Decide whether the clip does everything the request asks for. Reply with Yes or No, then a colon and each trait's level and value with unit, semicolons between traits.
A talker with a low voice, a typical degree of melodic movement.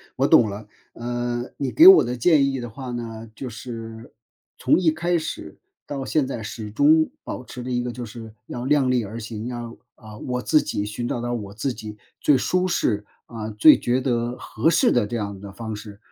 Yes: low, 120 Hz; average, 3.1 semitones